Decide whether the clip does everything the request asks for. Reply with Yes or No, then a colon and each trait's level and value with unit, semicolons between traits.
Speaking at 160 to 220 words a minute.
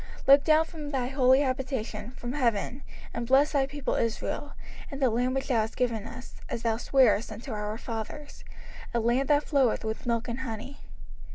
Yes: average, 190 wpm